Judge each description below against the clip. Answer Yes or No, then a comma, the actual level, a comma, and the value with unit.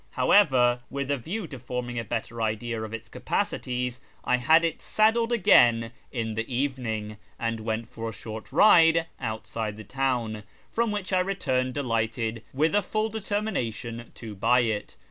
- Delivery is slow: No, average, 165 wpm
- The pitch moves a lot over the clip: Yes, wide, 6.1 semitones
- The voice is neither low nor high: No, low, 125 Hz